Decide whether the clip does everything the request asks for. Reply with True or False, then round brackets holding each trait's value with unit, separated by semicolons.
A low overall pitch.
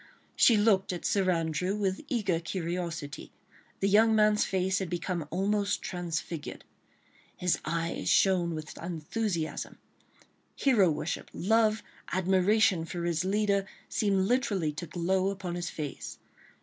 False (185 Hz)